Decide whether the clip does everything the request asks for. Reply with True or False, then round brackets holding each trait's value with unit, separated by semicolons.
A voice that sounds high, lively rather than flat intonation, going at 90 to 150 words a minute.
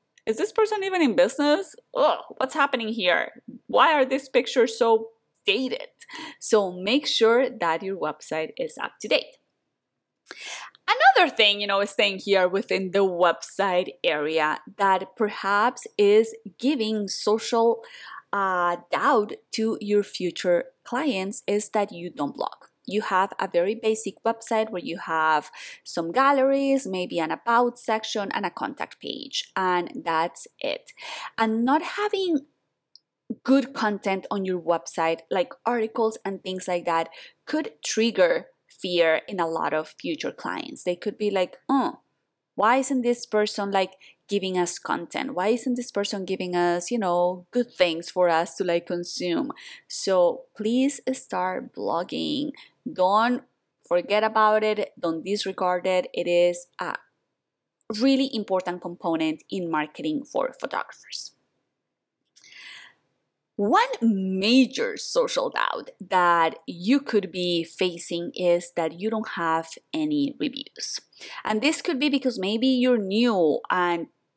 True (215 Hz; 6.6 semitones; 140 wpm)